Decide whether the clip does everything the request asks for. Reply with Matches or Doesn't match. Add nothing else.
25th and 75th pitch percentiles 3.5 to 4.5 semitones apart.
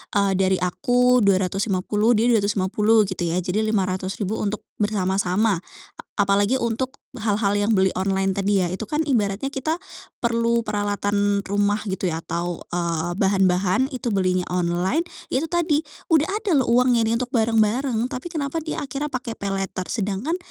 Matches